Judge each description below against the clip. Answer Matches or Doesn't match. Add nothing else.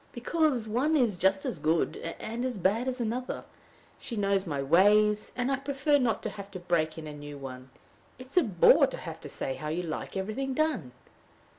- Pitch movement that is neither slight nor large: Doesn't match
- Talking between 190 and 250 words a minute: Matches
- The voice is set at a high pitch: Matches